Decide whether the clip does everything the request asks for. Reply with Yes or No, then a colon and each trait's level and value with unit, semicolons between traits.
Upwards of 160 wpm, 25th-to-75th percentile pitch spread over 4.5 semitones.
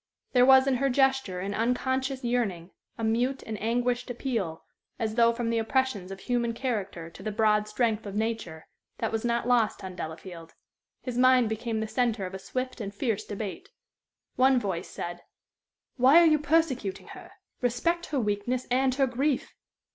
No: average, 175 wpm; average, 3.9 semitones